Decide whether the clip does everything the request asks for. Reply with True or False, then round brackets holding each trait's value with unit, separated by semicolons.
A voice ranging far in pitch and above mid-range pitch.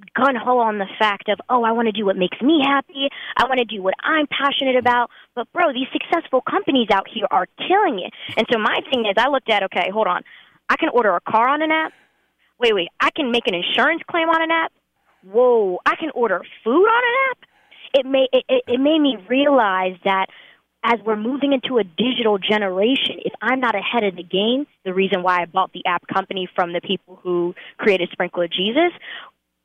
True (6.4 semitones; 240 Hz)